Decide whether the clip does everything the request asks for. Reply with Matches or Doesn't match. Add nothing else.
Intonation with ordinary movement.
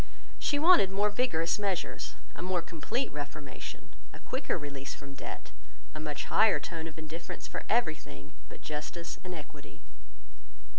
Matches